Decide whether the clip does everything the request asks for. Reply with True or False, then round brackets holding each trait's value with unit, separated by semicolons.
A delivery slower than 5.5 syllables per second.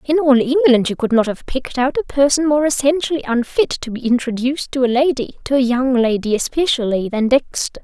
False (5.8 syllables/s)